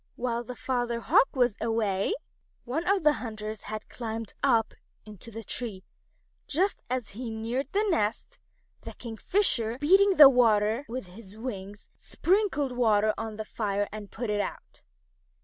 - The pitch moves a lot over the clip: No, average, 3.4 semitones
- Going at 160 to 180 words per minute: No, average, 150 wpm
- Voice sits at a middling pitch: No, high, 230 Hz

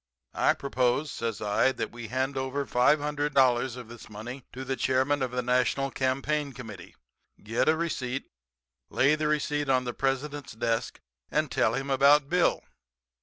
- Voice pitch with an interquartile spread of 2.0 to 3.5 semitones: Yes, average, 2.8 semitones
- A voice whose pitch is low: Yes, low, 130 Hz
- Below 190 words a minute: Yes, average, 160 wpm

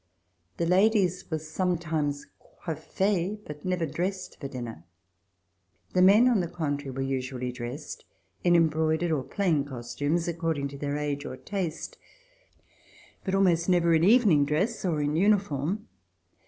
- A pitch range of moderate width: Yes, average, 4.4 semitones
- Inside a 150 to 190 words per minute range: No, average, 140 wpm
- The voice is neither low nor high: Yes, medium, 165 Hz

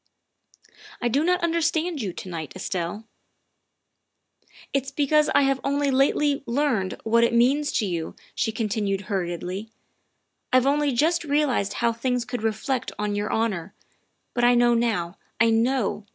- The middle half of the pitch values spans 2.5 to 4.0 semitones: No, average, 5.3 semitones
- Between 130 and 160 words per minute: No, average, 170 wpm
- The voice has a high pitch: Yes, high, 235 Hz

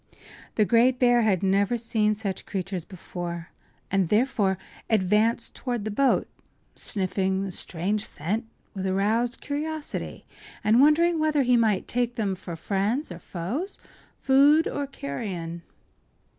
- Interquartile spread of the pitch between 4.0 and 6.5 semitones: Yes, average, 4.6 semitones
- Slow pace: Yes, slow, 130 wpm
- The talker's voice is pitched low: No, high, 215 Hz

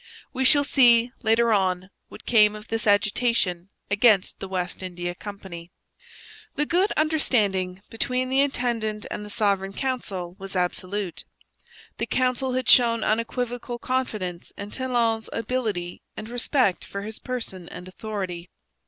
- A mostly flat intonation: No, average, 4.6 semitones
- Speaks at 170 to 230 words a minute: No, slow, 135 wpm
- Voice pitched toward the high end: Yes, high, 215 Hz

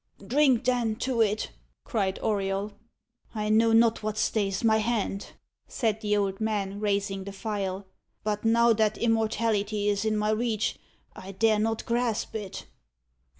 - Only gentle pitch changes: Yes, narrow, 1.9 semitones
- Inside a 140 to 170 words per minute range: Yes, average, 150 wpm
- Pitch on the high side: Yes, high, 215 Hz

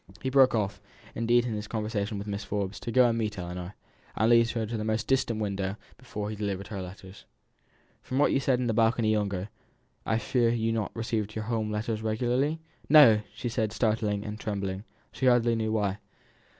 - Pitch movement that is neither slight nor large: No, narrow, 2.2 semitones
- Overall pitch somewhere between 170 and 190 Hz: No, low, 110 Hz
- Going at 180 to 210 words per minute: Yes, fast, 205 wpm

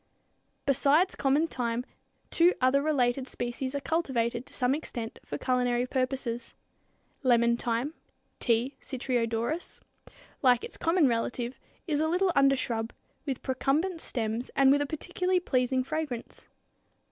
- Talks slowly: Yes, slow, 130 wpm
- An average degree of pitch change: Yes, average, 3.6 semitones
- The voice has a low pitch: No, very high, 260 Hz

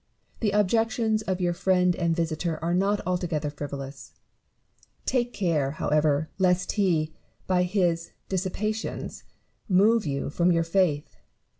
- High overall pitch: No, medium, 180 Hz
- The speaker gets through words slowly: Yes, slow, 125 wpm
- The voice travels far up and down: No, average, 3.7 semitones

